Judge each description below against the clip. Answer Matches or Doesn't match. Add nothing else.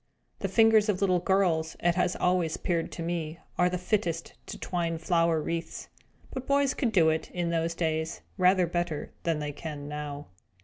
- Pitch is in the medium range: Matches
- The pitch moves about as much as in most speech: Doesn't match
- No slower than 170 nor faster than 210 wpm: Matches